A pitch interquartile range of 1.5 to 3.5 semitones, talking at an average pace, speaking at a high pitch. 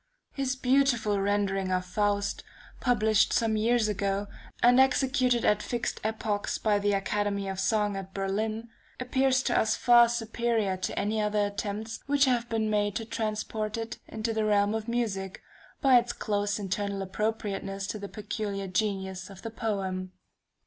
Yes: narrow, 2.5 semitones; average, 155 wpm; high, 215 Hz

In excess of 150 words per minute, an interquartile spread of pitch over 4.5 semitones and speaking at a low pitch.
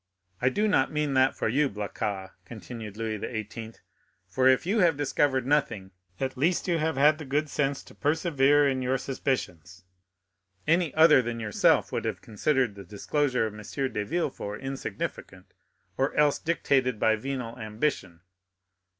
Yes: average, 160 wpm; average, 5.1 semitones; low, 130 Hz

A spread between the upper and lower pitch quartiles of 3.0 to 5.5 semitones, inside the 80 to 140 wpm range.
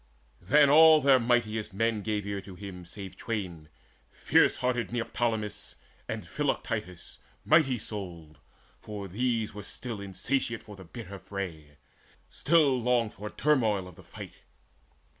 Yes: average, 4.3 semitones; slow, 135 wpm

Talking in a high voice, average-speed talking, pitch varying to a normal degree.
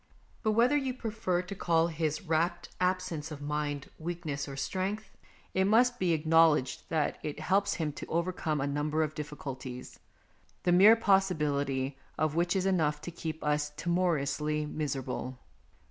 No: medium, 160 Hz; average, 160 wpm; average, 3.7 semitones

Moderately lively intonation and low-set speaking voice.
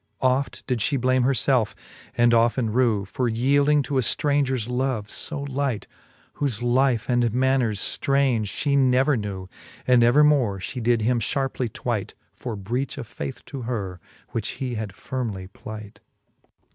Yes: average, 3.3 semitones; low, 125 Hz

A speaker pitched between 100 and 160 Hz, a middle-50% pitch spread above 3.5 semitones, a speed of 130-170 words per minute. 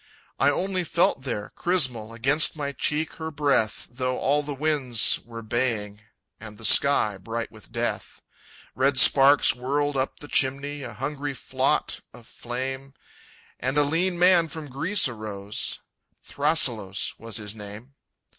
Yes: low, 135 Hz; average, 4.3 semitones; average, 145 wpm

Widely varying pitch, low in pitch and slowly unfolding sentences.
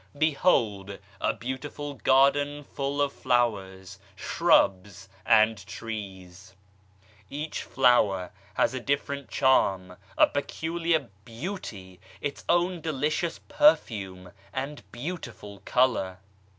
Yes: wide, 6.6 semitones; low, 125 Hz; slow, 95 wpm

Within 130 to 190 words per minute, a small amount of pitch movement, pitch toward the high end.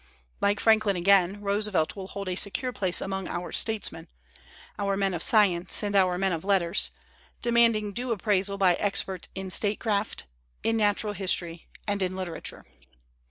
Yes: average, 155 wpm; narrow, 2.0 semitones; high, 200 Hz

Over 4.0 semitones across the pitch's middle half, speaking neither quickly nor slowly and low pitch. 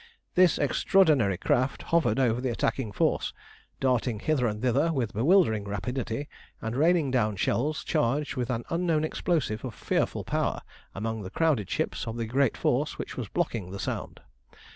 Yes: average, 5.3 semitones; average, 165 wpm; low, 125 Hz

